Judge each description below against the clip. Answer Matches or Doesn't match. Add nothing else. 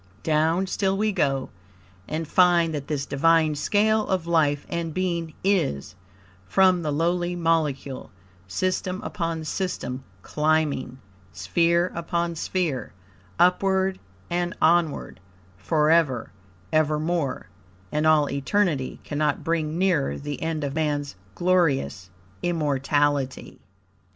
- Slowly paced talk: Matches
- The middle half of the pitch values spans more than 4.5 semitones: Doesn't match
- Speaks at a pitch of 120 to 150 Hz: Doesn't match